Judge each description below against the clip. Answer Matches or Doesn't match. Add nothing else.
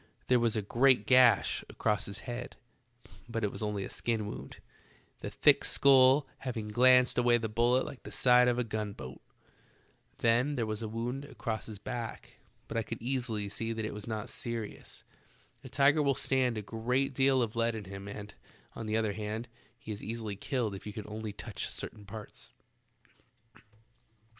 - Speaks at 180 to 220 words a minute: Matches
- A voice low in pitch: Matches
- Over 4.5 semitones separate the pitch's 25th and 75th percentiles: Doesn't match